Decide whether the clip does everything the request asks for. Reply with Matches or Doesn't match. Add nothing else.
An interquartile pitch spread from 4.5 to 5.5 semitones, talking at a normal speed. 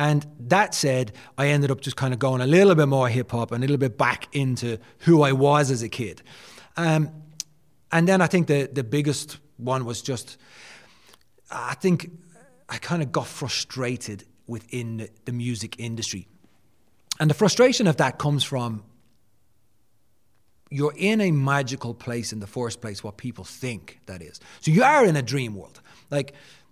Doesn't match